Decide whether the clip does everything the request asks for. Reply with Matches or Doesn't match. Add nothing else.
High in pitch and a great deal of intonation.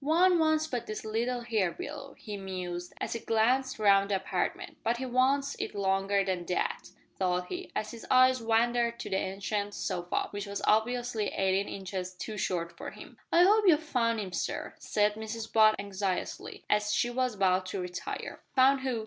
Doesn't match